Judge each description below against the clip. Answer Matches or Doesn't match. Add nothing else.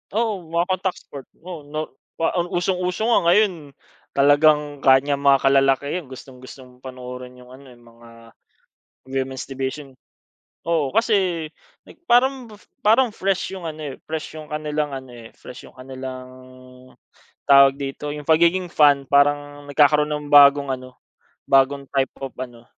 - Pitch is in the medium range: Matches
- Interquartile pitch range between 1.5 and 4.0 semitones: Matches